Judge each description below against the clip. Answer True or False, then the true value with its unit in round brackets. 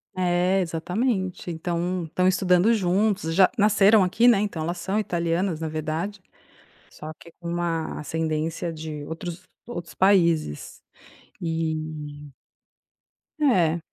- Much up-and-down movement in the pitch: False (2.9 semitones)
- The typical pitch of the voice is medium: True (175 Hz)